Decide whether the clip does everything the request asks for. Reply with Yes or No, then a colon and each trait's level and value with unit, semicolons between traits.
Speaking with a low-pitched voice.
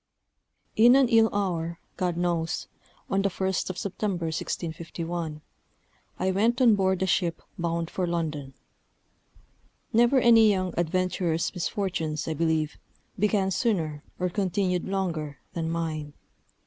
No: medium, 180 Hz